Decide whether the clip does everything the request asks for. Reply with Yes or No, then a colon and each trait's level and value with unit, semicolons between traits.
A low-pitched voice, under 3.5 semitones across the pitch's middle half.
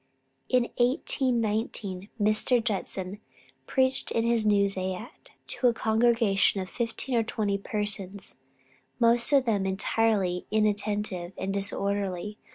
No: high, 210 Hz; average, 2.8 semitones